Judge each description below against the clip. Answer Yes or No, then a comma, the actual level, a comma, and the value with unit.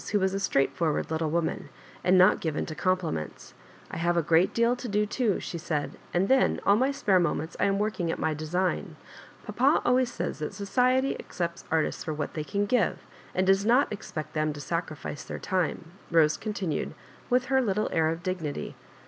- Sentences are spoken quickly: Yes, fast, 210 wpm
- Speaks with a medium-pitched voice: Yes, medium, 180 Hz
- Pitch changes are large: No, average, 4.7 semitones